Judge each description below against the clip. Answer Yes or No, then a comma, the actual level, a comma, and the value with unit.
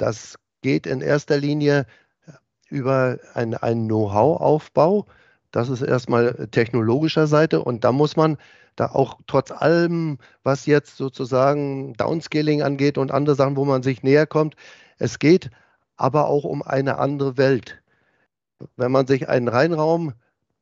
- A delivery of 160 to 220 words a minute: No, average, 140 wpm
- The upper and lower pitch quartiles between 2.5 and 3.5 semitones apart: Yes, average, 2.8 semitones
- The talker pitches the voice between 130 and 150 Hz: Yes, medium, 140 Hz